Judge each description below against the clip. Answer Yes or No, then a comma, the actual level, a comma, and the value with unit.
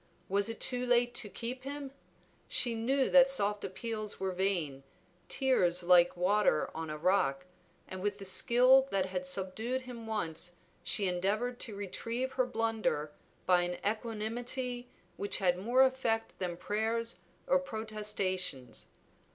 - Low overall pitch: No, high, 215 Hz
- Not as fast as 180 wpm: Yes, average, 145 wpm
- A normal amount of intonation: Yes, average, 4.8 semitones